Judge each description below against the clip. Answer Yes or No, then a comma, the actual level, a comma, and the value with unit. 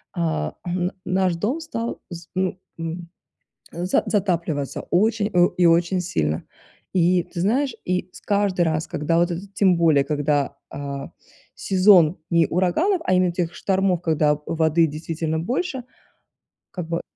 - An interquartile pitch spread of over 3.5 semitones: No, average, 2.8 semitones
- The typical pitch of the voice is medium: Yes, medium, 175 Hz